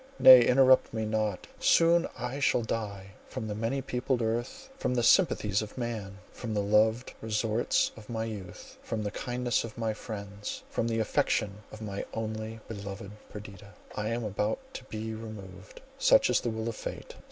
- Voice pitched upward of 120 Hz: No, low, 110 Hz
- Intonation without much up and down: Yes, narrow, 2.2 semitones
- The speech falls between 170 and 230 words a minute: Yes, average, 175 wpm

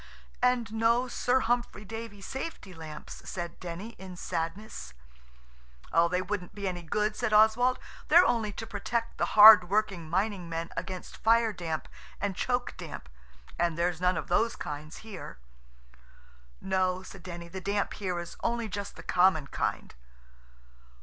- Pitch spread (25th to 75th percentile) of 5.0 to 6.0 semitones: No, average, 4.2 semitones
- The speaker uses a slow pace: No, average, 150 wpm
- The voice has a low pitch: No, high, 195 Hz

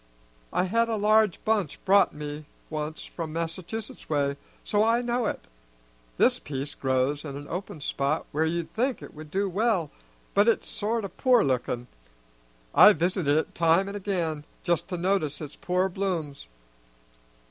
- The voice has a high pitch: No, medium, 175 Hz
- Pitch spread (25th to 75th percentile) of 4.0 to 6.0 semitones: Yes, average, 5.3 semitones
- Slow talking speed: No, average, 160 wpm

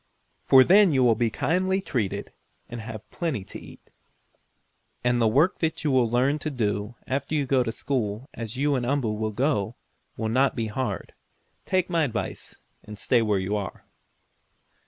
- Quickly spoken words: No, average, 175 wpm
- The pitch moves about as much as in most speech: Yes, average, 4.4 semitones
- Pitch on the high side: No, low, 125 Hz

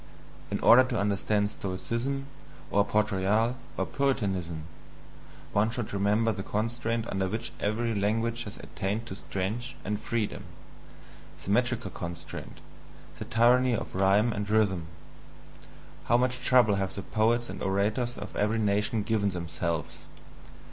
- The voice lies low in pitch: Yes, low, 105 Hz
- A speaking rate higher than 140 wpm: No, slow, 135 wpm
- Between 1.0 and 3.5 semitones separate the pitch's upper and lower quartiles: Yes, average, 2.9 semitones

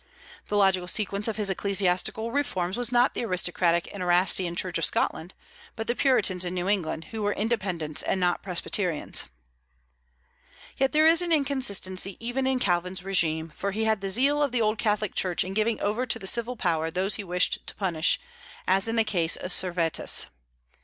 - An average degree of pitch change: Yes, average, 4.0 semitones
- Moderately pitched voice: No, high, 195 Hz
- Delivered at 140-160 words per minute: No, average, 185 wpm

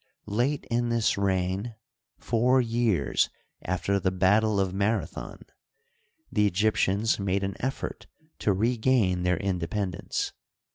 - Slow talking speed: Yes, slow, 125 wpm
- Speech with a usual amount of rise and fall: Yes, average, 3.5 semitones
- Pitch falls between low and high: No, low, 100 Hz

